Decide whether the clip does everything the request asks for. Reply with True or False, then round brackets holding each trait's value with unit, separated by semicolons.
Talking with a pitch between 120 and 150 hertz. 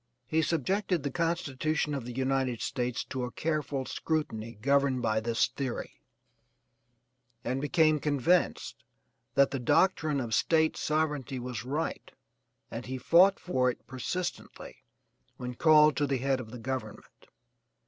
True (135 Hz)